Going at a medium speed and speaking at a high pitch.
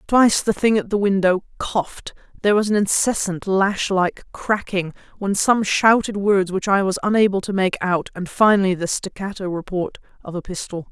Yes: average, 180 wpm; high, 195 Hz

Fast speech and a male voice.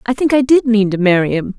No: fast, 305 wpm; female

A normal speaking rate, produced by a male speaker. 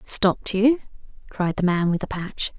No: average, 185 wpm; female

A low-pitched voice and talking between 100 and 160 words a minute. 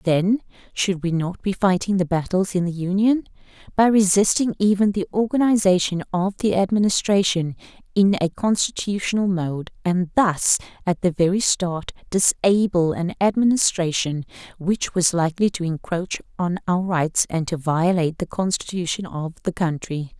No: medium, 185 Hz; average, 145 wpm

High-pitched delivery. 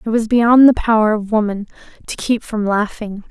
Yes: high, 220 Hz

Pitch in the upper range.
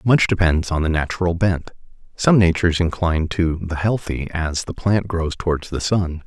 No: very low, 85 Hz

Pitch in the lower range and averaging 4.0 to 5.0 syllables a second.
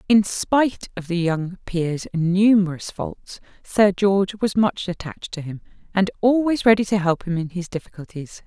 No: high, 190 Hz; 4.7 syllables/s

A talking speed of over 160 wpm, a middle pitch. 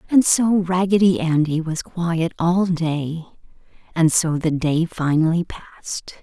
No: slow, 135 wpm; medium, 170 Hz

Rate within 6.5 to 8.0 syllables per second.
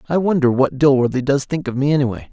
Yes: 6.6 syllables/s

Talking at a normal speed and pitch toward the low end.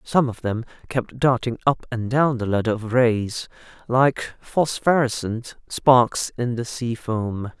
Yes: average, 150 wpm; low, 120 Hz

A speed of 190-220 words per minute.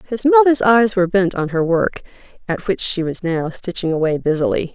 Yes: average, 200 wpm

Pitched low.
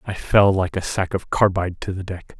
Yes: very low, 95 Hz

